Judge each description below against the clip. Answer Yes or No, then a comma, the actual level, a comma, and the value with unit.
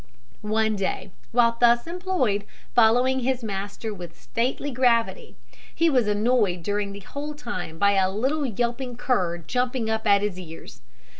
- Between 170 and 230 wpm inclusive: No, average, 150 wpm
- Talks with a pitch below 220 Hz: No, high, 230 Hz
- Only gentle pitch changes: No, average, 3.9 semitones